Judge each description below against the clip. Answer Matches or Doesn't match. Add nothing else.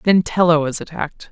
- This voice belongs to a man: Doesn't match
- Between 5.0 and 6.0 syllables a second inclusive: Matches